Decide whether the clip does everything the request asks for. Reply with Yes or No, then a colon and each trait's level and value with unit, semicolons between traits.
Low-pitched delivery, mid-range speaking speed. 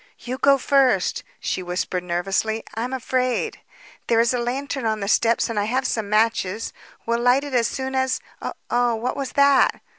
No: high, 235 Hz; average, 180 wpm